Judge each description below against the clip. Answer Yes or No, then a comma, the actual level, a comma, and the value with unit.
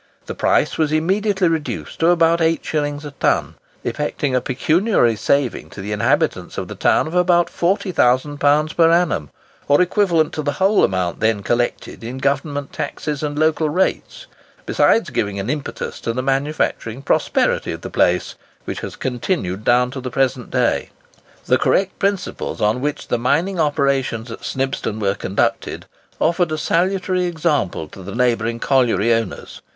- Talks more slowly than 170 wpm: Yes, average, 160 wpm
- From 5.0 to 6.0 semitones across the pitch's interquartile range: Yes, wide, 5.5 semitones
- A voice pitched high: No, medium, 145 Hz